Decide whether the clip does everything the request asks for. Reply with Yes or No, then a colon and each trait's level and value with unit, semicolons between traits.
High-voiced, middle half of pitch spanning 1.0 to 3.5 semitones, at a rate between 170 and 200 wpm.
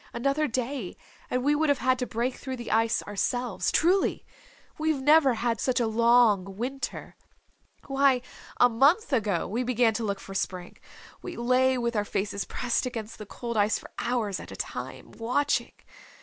Yes: high, 240 Hz; average, 3.1 semitones; average, 175 wpm